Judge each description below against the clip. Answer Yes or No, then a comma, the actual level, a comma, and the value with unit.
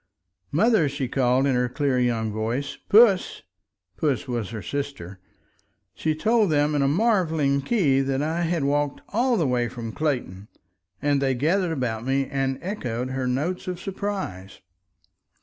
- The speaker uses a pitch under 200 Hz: Yes, medium, 140 Hz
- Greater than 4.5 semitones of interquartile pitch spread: Yes, average, 5.1 semitones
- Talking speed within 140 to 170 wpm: Yes, average, 155 wpm